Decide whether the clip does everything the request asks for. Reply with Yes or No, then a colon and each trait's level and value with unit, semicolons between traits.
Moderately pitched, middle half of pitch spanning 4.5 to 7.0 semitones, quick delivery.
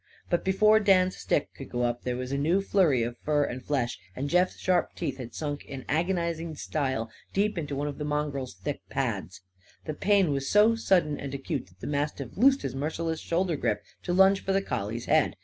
Yes: medium, 150 Hz; wide, 5.6 semitones; fast, 210 wpm